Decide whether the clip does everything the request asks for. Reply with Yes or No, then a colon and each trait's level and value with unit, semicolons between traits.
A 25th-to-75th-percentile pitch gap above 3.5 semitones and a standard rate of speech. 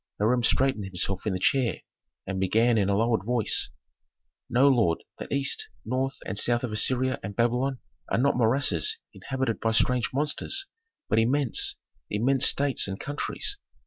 Yes: average, 4.0 semitones; average, 155 wpm